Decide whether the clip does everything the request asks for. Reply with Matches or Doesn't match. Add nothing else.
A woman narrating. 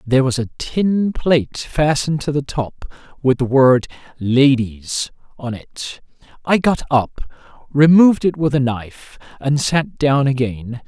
Doesn't match